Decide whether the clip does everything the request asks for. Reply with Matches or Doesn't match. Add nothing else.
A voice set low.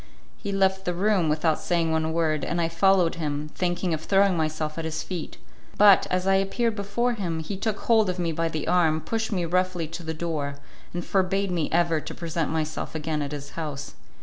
Doesn't match